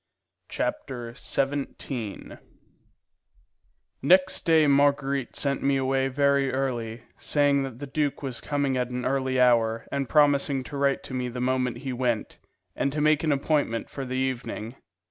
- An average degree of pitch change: No, narrow, 2.0 semitones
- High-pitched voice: No, low, 135 Hz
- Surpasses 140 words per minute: Yes, average, 150 wpm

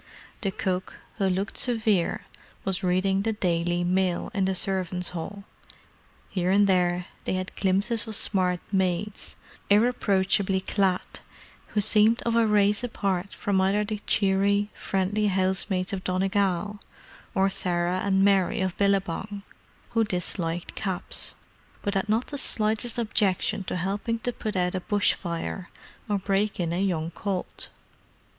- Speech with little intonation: Yes, narrow, 2.1 semitones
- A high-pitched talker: Yes, high, 195 Hz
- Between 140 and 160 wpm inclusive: Yes, average, 145 wpm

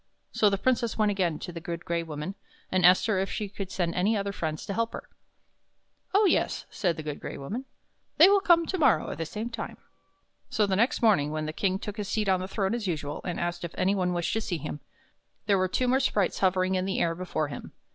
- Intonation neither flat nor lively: Yes, average, 4.1 semitones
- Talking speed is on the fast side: Yes, fast, 255 wpm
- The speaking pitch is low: No, high, 190 Hz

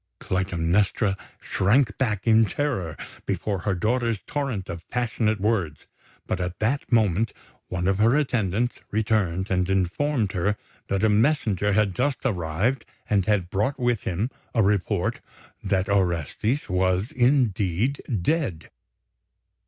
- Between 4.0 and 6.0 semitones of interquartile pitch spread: Yes, average, 4.3 semitones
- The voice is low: Yes, low, 105 Hz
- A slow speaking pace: Yes, slow, 130 wpm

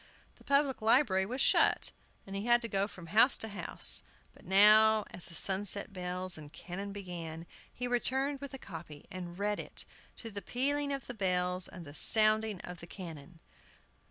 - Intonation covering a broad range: No, average, 4.3 semitones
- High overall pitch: Yes, high, 200 Hz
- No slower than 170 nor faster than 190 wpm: Yes, average, 180 wpm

